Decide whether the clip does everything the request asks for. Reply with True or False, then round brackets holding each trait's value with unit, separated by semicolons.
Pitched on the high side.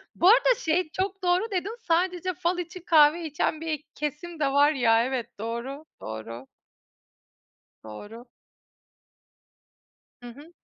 True (310 Hz)